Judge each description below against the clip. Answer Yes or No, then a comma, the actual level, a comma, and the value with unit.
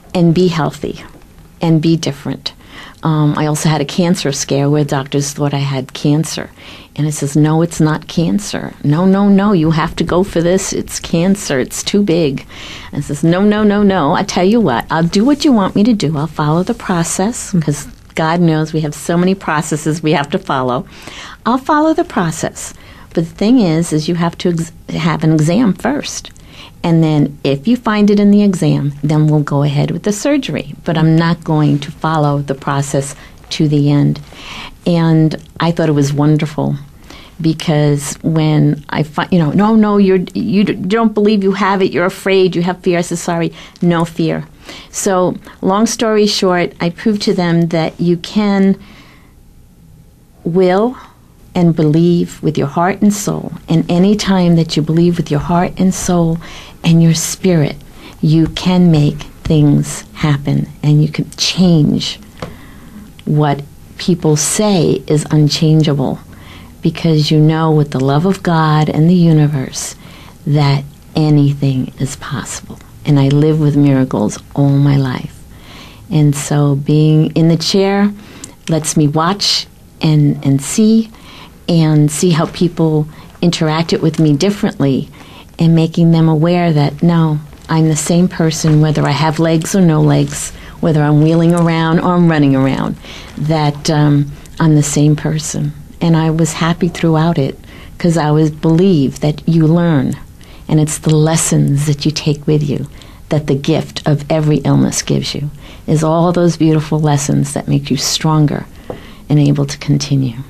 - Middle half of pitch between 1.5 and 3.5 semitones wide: Yes, average, 3.1 semitones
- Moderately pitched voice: Yes, medium, 160 Hz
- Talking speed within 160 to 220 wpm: Yes, average, 170 wpm